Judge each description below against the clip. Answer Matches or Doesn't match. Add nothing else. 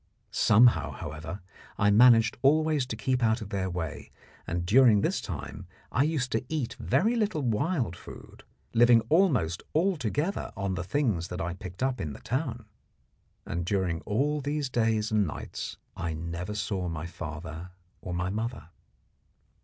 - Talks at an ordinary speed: Matches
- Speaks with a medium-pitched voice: Doesn't match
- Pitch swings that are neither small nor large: Doesn't match